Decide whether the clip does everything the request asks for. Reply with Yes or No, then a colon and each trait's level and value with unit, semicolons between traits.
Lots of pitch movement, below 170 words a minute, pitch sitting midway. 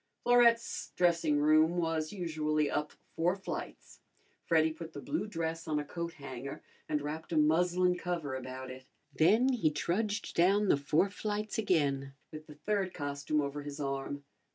No: average, 3.7 semitones; average, 160 wpm; medium, 160 Hz